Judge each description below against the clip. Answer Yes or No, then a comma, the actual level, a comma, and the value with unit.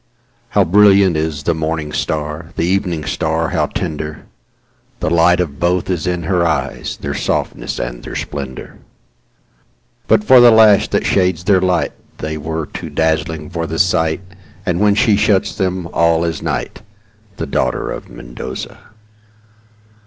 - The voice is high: No, very low, 85 Hz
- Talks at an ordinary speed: No, slow, 130 wpm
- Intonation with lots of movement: No, average, 3.1 semitones